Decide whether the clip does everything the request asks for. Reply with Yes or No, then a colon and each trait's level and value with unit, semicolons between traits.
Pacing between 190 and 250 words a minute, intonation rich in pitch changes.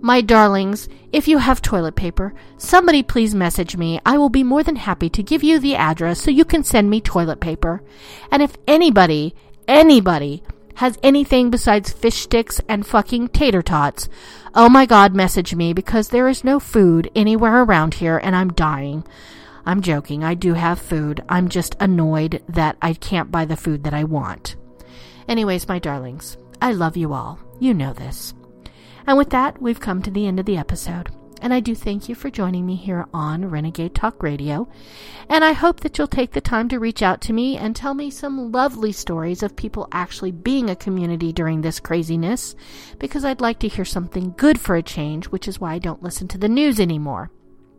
Yes: average, 200 wpm; wide, 6.9 semitones